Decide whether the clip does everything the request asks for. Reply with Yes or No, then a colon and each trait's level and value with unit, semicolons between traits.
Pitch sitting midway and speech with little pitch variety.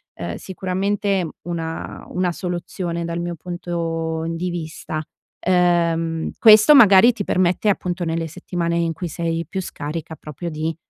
Yes: medium, 170 Hz; narrow, 1.9 semitones